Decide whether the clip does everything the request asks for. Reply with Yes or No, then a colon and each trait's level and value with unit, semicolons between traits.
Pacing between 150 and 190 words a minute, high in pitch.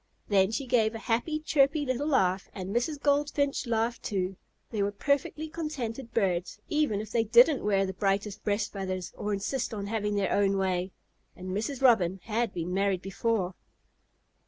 Yes: average, 170 wpm; high, 215 Hz